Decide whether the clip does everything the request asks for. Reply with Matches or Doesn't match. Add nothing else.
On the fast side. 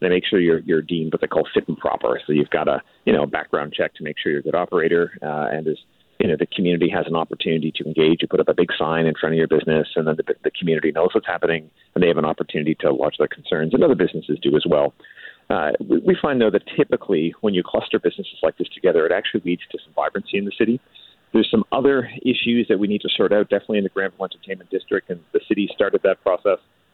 Matches